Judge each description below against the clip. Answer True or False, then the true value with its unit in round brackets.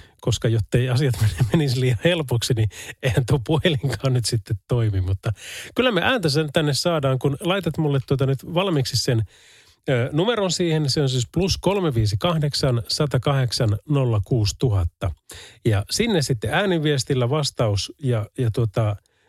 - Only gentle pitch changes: False (4.8 semitones)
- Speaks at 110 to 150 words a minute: True (135 wpm)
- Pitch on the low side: True (130 Hz)